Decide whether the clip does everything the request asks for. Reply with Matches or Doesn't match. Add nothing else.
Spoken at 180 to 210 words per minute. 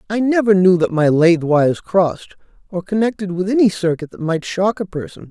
Matches